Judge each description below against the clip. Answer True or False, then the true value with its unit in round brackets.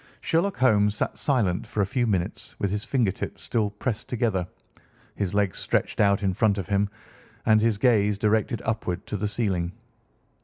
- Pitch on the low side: True (105 Hz)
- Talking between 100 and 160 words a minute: False (175 wpm)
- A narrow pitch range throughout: True (2.3 semitones)